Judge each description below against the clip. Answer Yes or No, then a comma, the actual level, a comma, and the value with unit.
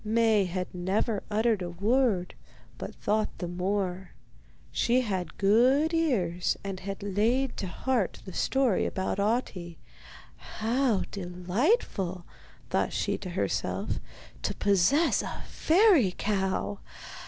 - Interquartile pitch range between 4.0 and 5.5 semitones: Yes, average, 4.7 semitones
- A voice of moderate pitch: No, high, 200 Hz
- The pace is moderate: No, slow, 120 wpm